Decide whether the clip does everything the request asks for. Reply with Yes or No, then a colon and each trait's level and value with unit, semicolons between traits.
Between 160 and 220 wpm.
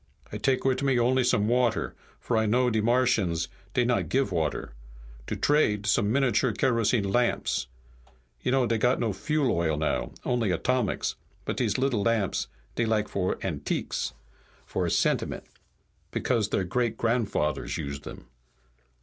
No: average, 150 wpm